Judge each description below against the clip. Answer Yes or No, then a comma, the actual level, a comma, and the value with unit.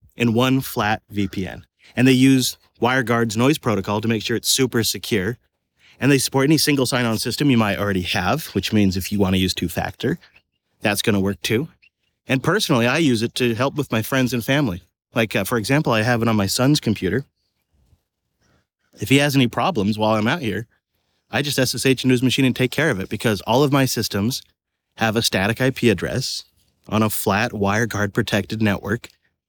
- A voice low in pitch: Yes, low, 115 Hz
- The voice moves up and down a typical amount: Yes, average, 4.2 semitones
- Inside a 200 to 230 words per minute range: Yes, fast, 205 wpm